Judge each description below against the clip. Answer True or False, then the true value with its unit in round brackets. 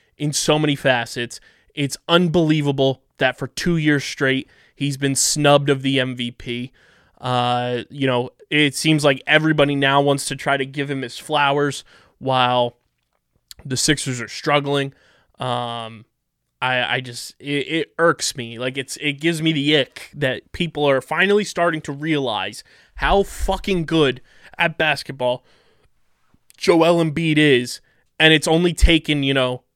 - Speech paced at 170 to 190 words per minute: False (150 wpm)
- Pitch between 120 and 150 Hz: True (140 Hz)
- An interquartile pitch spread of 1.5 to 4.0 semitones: True (3.3 semitones)